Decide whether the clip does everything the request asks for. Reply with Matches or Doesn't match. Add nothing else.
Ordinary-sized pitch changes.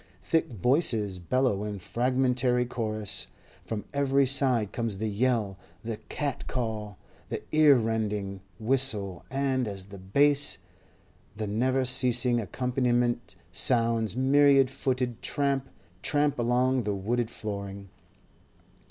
Matches